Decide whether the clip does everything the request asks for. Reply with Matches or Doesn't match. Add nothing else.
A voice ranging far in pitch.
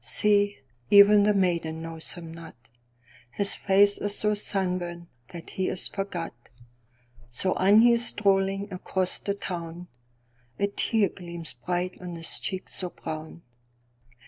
Doesn't match